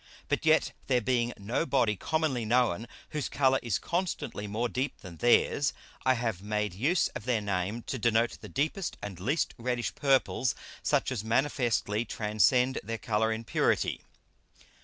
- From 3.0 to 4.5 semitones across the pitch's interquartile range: Yes, average, 3.8 semitones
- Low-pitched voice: Yes, low, 120 Hz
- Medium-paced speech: Yes, average, 160 wpm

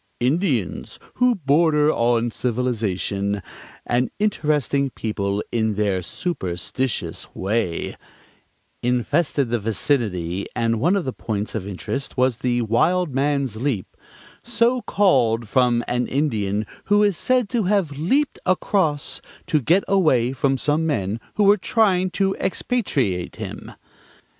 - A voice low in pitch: Yes, low, 130 Hz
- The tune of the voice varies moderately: No, wide, 7.7 semitones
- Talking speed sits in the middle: No, slow, 125 wpm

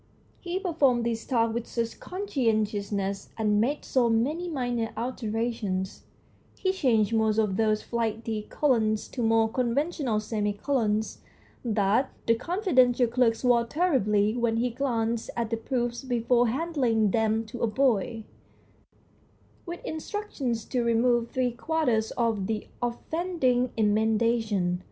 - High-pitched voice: Yes, high, 235 Hz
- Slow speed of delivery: Yes, slow, 125 wpm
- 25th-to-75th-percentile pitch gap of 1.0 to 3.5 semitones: Yes, narrow, 2.6 semitones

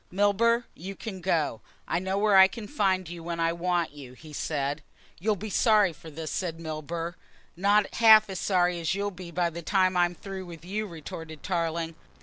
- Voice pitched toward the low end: No, medium, 175 Hz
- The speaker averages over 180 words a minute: Yes, average, 195 wpm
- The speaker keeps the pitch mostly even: No, average, 3.2 semitones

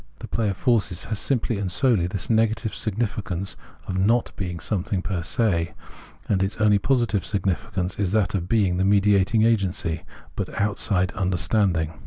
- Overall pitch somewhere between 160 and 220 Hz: No, low, 100 Hz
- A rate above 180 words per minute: No, average, 160 wpm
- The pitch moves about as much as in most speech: Yes, average, 3.2 semitones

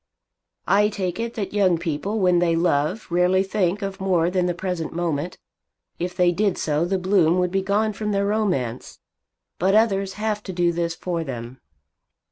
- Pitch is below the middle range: No, medium, 180 Hz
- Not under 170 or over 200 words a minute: Yes, average, 180 wpm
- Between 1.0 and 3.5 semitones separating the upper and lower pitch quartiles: Yes, average, 2.7 semitones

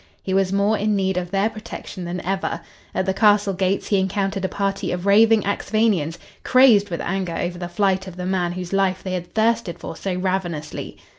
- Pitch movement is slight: Yes, narrow, 1.9 semitones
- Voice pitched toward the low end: No, high, 190 Hz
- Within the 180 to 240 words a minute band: Yes, fast, 205 wpm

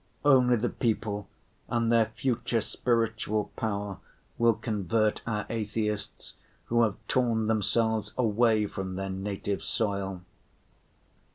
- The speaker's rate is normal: No, slow, 110 wpm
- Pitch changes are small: Yes, narrow, 2.2 semitones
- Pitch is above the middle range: No, low, 110 Hz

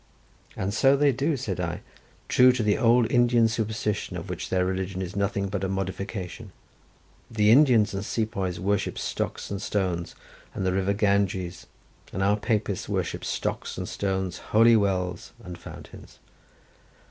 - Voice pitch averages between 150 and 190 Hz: No, low, 100 Hz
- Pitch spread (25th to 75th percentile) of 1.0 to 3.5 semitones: Yes, average, 3.1 semitones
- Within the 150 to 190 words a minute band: Yes, average, 155 wpm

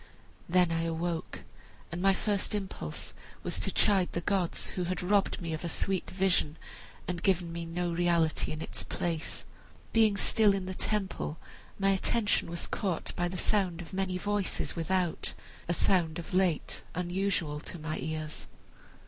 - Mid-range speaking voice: Yes, medium, 180 Hz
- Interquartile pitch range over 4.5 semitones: No, narrow, 2.5 semitones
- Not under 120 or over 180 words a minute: Yes, average, 165 wpm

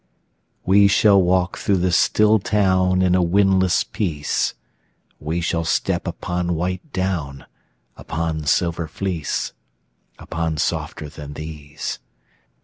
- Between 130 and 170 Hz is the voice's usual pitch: No, very low, 90 Hz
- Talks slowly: Yes, slow, 115 wpm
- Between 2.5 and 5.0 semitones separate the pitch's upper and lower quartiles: Yes, average, 2.9 semitones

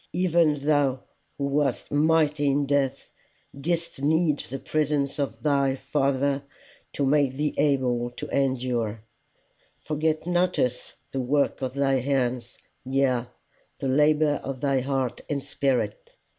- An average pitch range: No, narrow, 2.1 semitones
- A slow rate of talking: Yes, slow, 130 wpm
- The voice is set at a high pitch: No, medium, 140 Hz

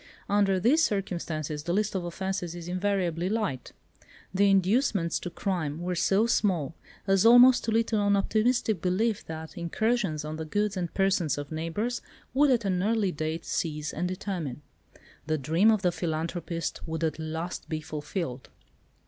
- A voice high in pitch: No, medium, 180 Hz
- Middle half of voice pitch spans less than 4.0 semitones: No, average, 4.3 semitones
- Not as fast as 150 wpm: No, average, 165 wpm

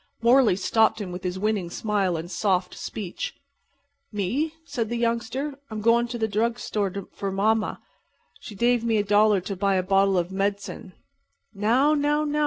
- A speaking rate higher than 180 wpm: No, average, 175 wpm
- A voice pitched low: No, high, 210 Hz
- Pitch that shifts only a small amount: No, average, 3.4 semitones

